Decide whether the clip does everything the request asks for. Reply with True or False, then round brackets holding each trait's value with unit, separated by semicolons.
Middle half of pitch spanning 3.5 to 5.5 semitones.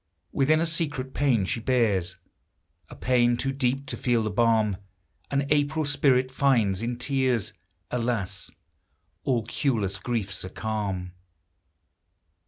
True (4.1 semitones)